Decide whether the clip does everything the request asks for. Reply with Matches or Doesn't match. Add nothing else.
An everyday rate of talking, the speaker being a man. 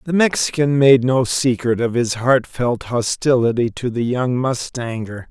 Matches